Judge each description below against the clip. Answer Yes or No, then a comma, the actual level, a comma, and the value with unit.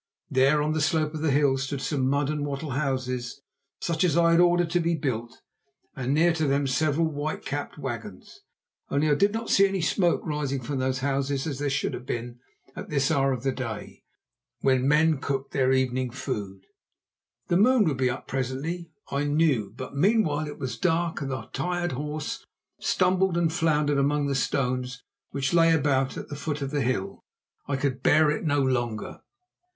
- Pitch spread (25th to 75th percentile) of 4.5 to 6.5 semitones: No, average, 3.2 semitones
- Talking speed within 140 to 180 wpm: No, average, 190 wpm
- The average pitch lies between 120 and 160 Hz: Yes, medium, 140 Hz